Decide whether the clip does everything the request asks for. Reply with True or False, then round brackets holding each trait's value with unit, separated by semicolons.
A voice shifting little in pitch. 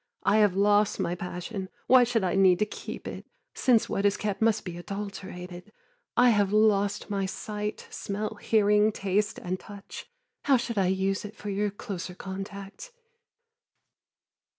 True (1.8 semitones)